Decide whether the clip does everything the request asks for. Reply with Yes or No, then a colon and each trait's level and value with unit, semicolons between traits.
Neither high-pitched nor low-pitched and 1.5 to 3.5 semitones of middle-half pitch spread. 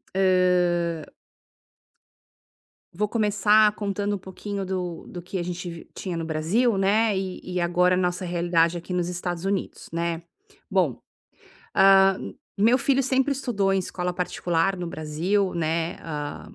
Yes: medium, 180 Hz; narrow, 2.6 semitones